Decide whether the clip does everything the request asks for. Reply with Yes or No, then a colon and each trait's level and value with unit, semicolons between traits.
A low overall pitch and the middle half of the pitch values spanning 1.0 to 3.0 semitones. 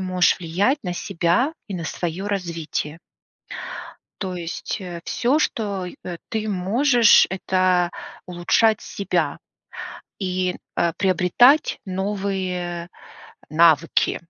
No: medium, 185 Hz; average, 2.7 semitones